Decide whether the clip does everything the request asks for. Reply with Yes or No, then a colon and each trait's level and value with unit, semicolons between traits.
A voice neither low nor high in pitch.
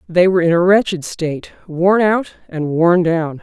Yes: medium, 175 Hz